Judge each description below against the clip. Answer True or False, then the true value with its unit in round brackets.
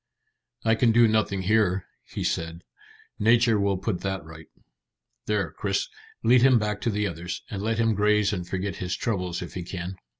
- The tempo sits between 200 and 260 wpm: False (180 wpm)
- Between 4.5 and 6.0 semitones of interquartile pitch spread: False (3.7 semitones)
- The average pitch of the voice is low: True (100 Hz)